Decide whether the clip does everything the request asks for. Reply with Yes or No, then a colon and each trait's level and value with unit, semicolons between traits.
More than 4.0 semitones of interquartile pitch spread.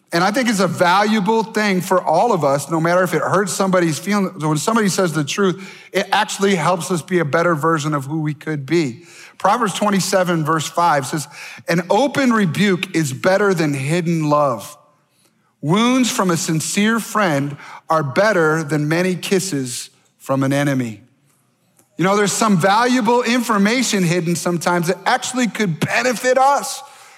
Yes: average, 4.6 semitones